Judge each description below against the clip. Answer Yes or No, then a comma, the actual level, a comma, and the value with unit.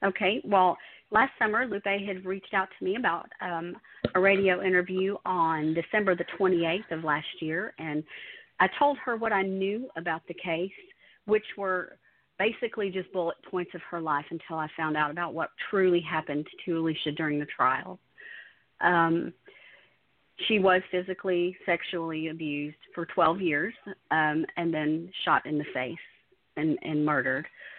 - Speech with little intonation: No, average, 3.3 semitones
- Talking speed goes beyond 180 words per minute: No, average, 160 wpm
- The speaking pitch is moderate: Yes, medium, 175 Hz